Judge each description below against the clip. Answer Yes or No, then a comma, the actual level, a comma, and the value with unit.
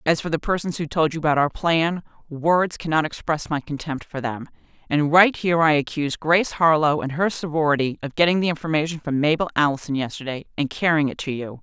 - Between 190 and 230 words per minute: Yes, fast, 205 wpm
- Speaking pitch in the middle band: Yes, medium, 155 Hz